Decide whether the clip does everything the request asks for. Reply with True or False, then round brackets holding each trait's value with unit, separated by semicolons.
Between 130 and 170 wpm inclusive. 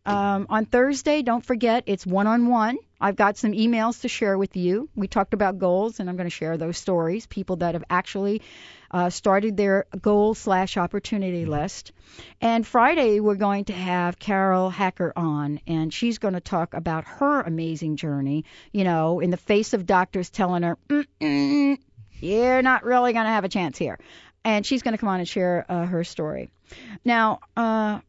False (185 wpm)